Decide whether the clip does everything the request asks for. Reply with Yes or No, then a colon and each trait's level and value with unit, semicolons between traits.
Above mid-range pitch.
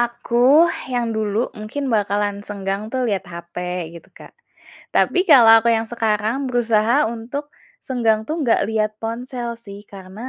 Yes: high, 225 Hz